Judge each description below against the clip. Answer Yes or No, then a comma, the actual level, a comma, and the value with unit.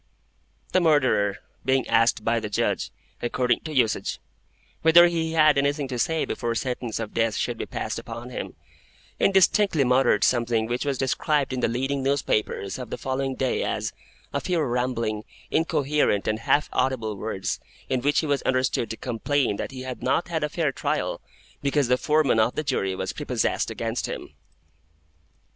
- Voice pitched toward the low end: Yes, low, 130 Hz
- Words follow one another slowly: No, average, 170 wpm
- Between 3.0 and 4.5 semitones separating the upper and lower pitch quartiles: Yes, average, 4.1 semitones